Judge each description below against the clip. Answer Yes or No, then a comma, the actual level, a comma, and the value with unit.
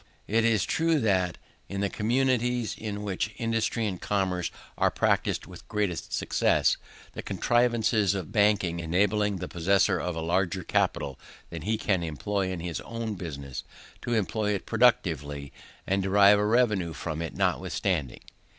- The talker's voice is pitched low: Yes, low, 100 Hz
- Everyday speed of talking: Yes, average, 150 wpm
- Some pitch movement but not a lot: Yes, average, 4.1 semitones